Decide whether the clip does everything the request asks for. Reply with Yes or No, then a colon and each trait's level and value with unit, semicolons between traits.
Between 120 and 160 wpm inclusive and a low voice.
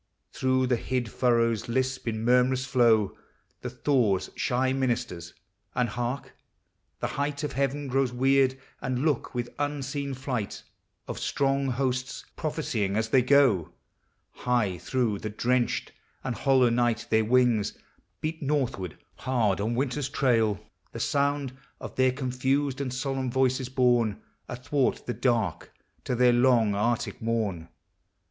Yes: slow, 135 wpm; low, 125 Hz